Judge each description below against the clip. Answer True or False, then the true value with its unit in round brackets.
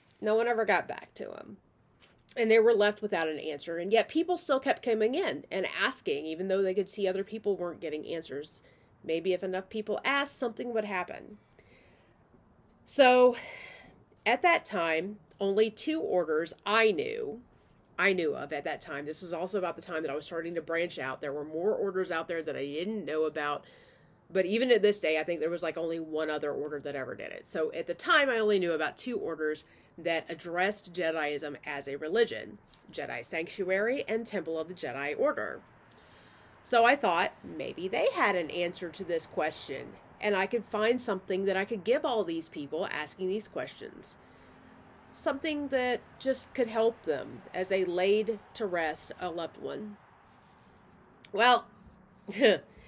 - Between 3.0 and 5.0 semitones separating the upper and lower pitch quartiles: False (5.6 semitones)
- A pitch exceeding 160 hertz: True (190 Hz)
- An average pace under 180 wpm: False (185 wpm)